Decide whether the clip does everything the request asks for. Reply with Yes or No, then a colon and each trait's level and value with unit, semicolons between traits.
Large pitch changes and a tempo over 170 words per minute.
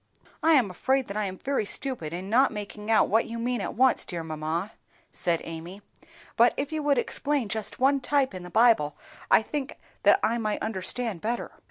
Yes: wide, 5.7 semitones; average, 200 wpm